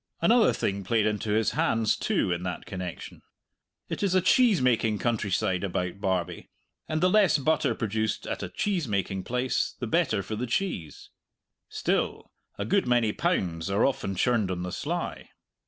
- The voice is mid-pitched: No, low, 110 Hz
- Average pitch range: No, wide, 6.7 semitones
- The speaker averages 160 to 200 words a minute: Yes, average, 170 wpm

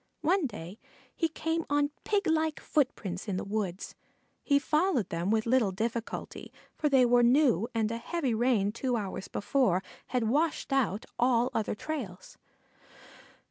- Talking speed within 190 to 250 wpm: No, average, 145 wpm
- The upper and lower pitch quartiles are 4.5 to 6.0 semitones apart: Yes, wide, 5.6 semitones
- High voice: Yes, high, 240 Hz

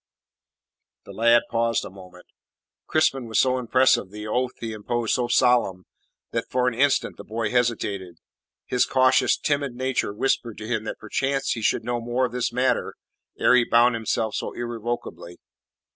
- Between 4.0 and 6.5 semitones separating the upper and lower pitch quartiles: No, narrow, 2.4 semitones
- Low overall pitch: Yes, low, 120 Hz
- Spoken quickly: No, average, 165 wpm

